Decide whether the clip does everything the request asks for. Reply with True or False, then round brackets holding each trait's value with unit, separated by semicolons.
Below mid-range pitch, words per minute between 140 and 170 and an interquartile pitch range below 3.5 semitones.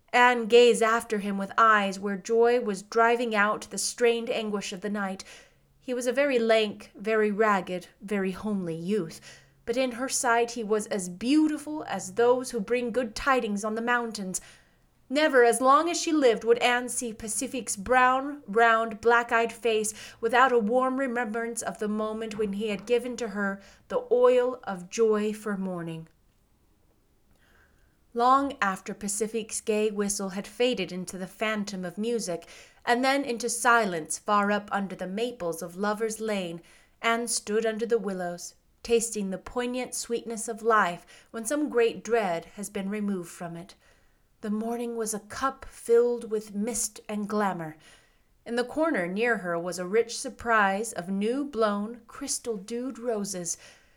False (225 Hz; 165 wpm; 3.1 semitones)